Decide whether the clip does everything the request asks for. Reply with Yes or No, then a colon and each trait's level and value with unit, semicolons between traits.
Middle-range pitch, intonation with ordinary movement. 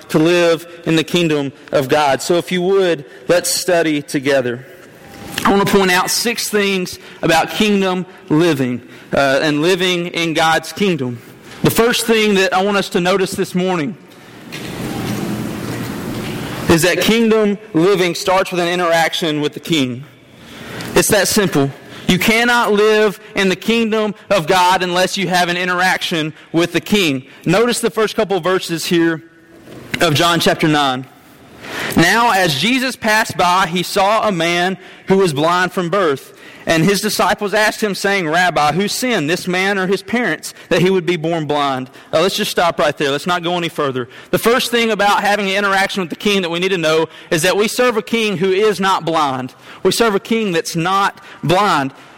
Yes: medium, 180 Hz; average, 3.6 semitones